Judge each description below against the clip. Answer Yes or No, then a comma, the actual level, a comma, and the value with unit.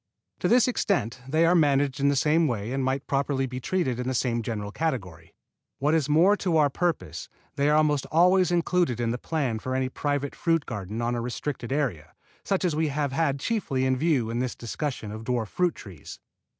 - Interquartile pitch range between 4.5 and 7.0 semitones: Yes, average, 5.0 semitones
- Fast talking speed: Yes, fast, 210 wpm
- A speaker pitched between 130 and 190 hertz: Yes, low, 135 Hz